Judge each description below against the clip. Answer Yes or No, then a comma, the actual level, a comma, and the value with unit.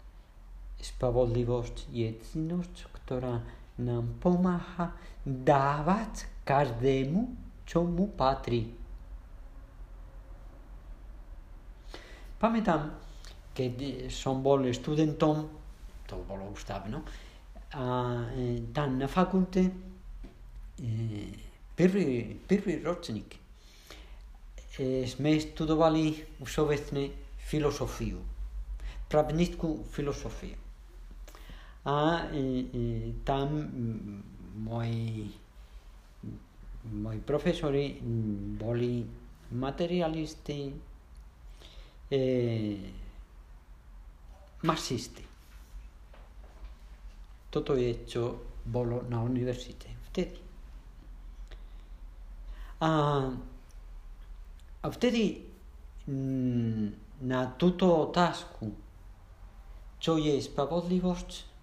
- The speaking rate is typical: No, slow, 60 wpm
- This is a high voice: No, low, 120 Hz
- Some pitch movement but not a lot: No, wide, 8.5 semitones